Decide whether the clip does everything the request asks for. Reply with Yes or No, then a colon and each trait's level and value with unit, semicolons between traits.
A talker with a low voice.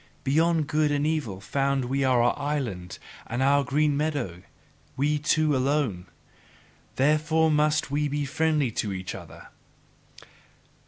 No: medium, 145 Hz